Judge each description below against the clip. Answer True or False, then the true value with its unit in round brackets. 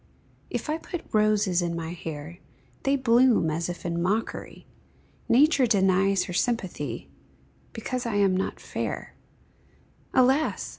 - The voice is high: True (200 Hz)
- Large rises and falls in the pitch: True (6.1 semitones)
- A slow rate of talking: True (130 wpm)